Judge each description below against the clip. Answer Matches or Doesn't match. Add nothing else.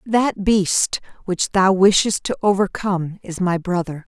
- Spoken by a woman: Matches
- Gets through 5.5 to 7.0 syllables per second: Doesn't match